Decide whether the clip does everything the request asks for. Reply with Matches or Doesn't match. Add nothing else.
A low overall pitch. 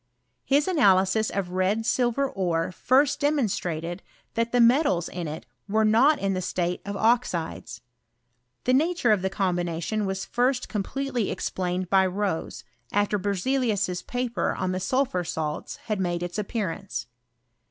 Doesn't match